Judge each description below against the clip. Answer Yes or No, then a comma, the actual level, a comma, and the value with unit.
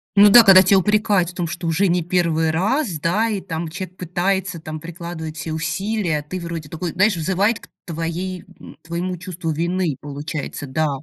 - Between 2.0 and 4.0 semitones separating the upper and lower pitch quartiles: Yes, average, 2.8 semitones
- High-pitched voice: No, medium, 175 Hz